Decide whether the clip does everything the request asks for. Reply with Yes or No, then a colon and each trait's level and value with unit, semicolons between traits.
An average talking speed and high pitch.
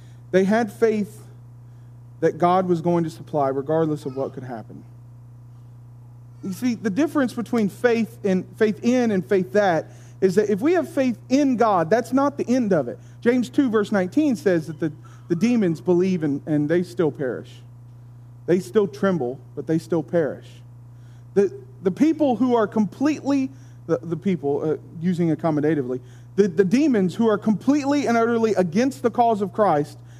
No: average, 175 wpm; medium, 175 Hz